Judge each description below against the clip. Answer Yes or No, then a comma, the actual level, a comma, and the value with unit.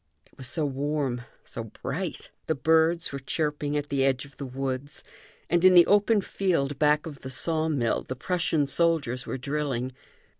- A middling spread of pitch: Yes, average, 3.3 semitones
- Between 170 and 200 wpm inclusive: Yes, average, 180 wpm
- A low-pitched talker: No, medium, 145 Hz